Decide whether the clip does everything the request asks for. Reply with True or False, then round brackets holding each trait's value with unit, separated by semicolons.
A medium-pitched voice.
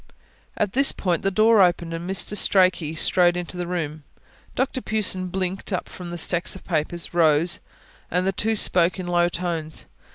True (180 Hz)